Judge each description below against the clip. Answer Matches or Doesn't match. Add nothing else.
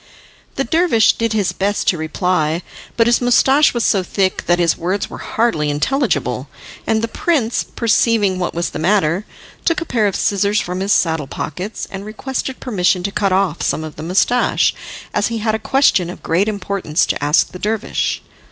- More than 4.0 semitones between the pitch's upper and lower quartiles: Matches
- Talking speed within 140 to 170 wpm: Doesn't match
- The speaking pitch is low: Doesn't match